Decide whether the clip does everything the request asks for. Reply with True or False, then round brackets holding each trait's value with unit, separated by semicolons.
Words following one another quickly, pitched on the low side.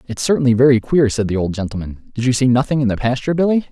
True (260 wpm; 125 Hz)